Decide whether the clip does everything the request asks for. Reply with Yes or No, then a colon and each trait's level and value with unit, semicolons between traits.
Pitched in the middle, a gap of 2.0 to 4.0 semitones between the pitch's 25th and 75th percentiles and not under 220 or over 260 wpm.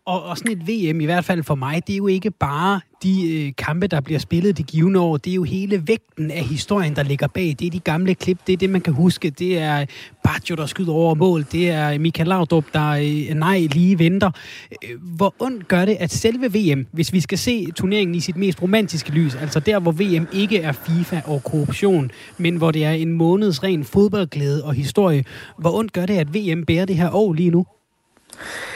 Yes: medium, 170 Hz; average, 3.4 semitones; fast, 225 wpm